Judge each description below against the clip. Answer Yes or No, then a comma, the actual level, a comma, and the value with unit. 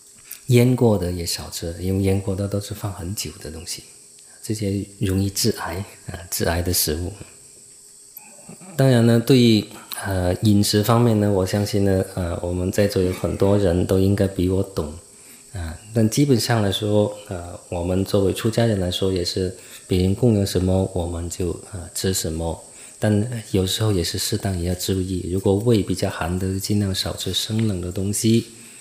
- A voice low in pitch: Yes, low, 100 Hz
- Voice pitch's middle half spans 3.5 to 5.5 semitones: No, narrow, 2.6 semitones